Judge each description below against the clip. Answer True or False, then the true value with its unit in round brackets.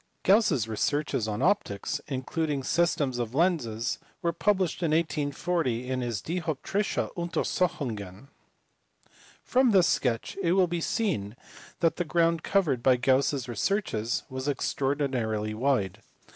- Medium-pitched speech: True (145 Hz)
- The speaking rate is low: True (130 wpm)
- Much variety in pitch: True (6.1 semitones)